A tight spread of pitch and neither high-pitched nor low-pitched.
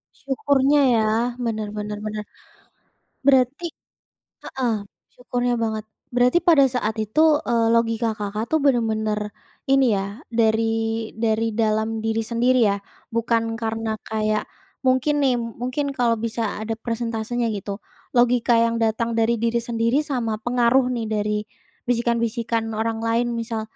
No: narrow, 1.9 semitones; high, 230 Hz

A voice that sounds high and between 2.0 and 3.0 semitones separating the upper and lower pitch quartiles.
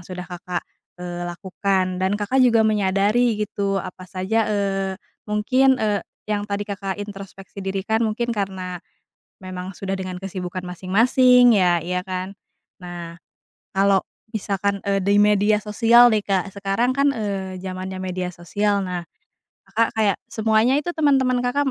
Yes: high, 200 Hz; average, 2.7 semitones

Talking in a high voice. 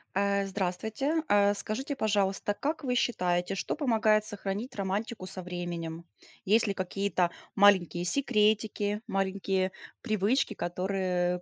Yes: high, 200 Hz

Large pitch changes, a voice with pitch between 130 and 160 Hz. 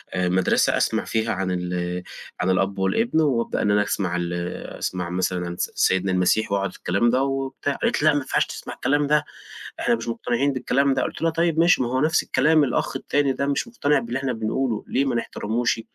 No: wide, 6.9 semitones; low, 120 Hz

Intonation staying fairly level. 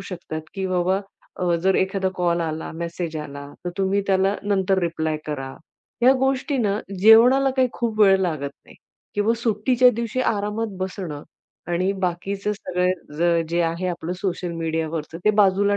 No: average, 3.5 semitones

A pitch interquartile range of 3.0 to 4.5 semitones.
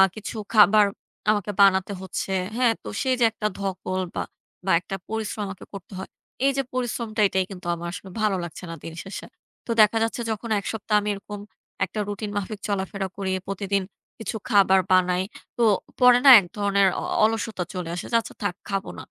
No: narrow, 2.4 semitones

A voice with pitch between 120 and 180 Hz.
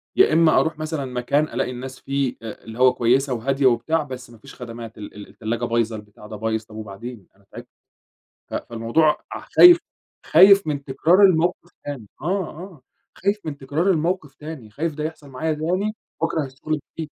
Yes: medium, 140 Hz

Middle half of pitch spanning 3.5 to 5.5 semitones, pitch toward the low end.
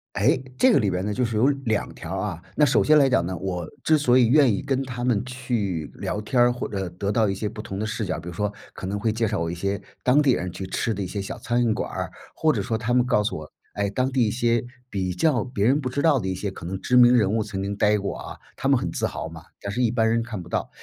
Yes: average, 4.2 semitones; low, 110 Hz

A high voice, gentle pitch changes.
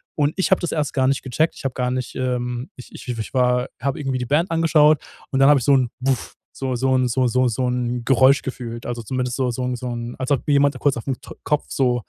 No: low, 130 Hz; narrow, 2.0 semitones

